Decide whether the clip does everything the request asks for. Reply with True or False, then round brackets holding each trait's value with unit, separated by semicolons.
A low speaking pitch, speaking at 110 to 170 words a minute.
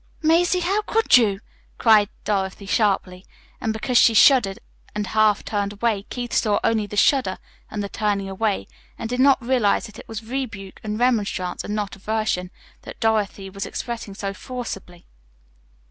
False (215 Hz; 160 wpm)